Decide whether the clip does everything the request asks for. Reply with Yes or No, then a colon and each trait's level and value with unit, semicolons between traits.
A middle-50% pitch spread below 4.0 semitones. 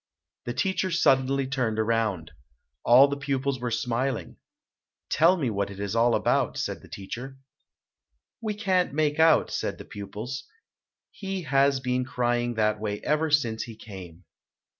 No: average, 4.4 semitones